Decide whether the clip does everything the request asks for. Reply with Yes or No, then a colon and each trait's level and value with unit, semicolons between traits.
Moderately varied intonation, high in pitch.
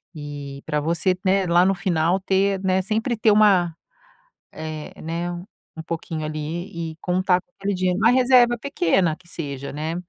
No: average, 3.6 semitones; medium, 180 Hz